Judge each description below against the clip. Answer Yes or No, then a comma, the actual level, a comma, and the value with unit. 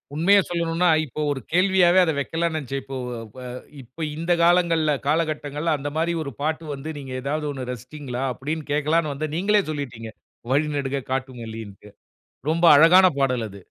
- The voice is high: No, medium, 150 Hz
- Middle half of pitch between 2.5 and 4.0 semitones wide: Yes, average, 3.7 semitones